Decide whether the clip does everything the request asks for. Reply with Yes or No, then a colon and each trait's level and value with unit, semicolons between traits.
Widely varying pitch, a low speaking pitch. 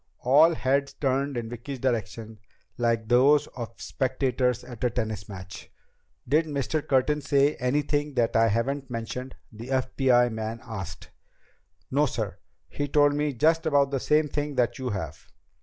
No: average, 3.7 semitones; low, 130 Hz